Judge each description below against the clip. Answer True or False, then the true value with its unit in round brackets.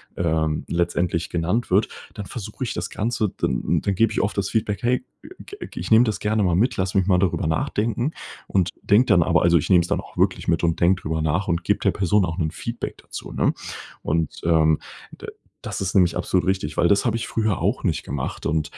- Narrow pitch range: False (4.0 semitones)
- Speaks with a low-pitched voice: True (95 Hz)